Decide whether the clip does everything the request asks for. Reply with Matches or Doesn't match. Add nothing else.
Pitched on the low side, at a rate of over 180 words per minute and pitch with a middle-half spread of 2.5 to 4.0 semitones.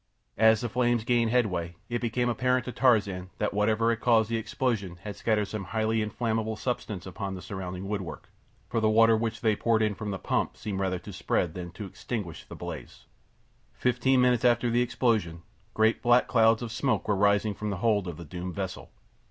Matches